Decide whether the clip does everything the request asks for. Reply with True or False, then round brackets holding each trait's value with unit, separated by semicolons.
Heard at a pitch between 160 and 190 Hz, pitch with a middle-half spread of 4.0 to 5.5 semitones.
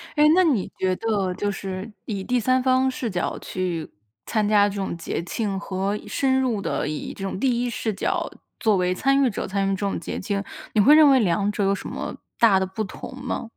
False (205 Hz; 4.5 semitones)